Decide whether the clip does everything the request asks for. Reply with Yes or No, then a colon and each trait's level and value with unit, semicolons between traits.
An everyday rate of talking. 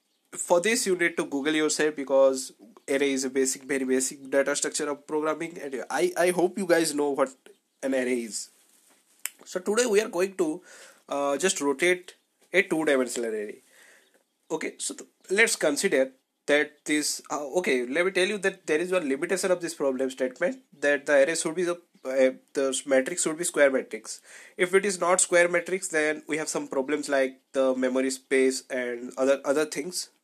Yes: average, 190 wpm